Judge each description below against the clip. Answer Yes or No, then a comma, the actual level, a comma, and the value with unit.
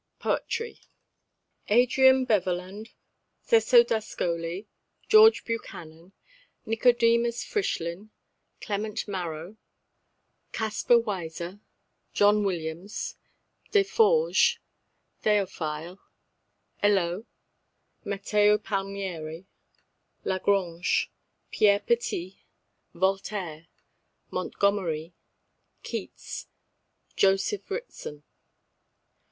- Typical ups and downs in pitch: Yes, average, 4.7 semitones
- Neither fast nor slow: No, slow, 60 wpm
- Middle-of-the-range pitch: No, high, 200 Hz